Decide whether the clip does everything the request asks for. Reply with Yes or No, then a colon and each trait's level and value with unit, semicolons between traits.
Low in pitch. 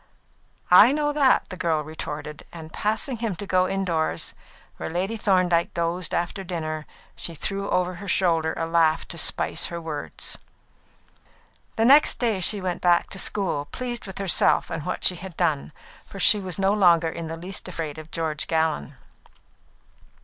No: medium, 175 Hz